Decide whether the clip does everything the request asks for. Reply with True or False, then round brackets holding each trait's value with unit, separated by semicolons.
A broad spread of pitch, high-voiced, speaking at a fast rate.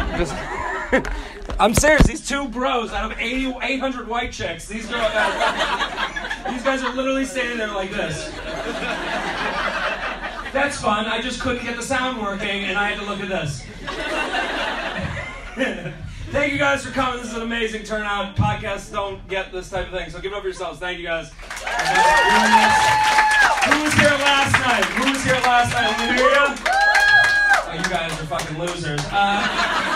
False (5.7 semitones; 235 Hz; 165 wpm)